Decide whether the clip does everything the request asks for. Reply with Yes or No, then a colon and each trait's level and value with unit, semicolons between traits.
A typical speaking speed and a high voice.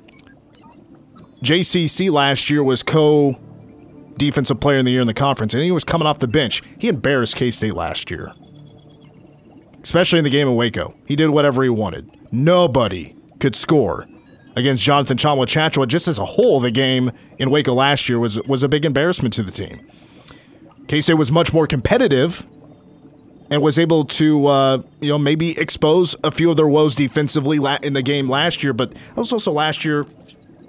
No: average, 175 wpm; medium, 145 Hz